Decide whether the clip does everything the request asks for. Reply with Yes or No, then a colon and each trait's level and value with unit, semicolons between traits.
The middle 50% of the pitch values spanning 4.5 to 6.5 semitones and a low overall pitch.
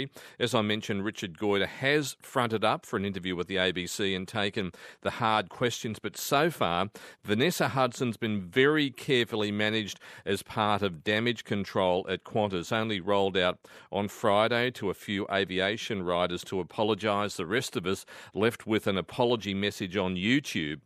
No: average, 2.7 semitones; low, 105 Hz